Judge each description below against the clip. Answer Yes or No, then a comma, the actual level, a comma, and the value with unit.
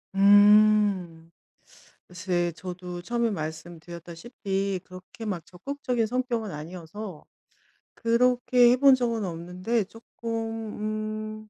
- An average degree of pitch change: Yes, average, 4.3 semitones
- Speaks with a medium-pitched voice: No, high, 205 Hz